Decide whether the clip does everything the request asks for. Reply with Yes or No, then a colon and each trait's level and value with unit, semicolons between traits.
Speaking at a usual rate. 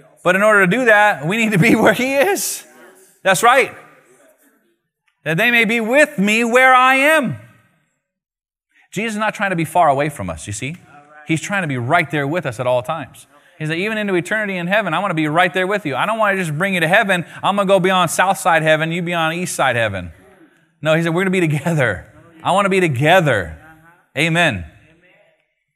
No: fast, 230 wpm